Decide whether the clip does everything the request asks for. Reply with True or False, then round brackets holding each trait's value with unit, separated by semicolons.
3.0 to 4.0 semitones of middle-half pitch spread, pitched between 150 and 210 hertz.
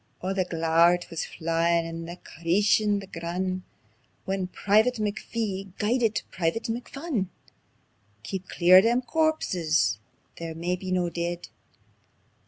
True (3.7 semitones; 185 Hz)